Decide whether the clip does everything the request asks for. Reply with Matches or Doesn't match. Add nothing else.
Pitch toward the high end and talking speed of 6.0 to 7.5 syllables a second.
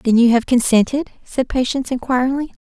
Matches